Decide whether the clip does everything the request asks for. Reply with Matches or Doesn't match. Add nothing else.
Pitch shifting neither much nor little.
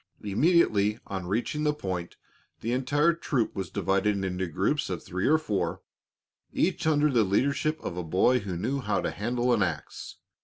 Doesn't match